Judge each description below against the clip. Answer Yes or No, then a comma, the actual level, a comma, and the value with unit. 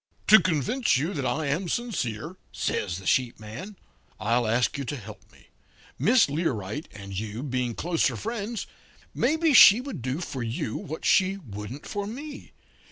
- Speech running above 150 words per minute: Yes, average, 165 wpm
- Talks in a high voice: No, medium, 145 Hz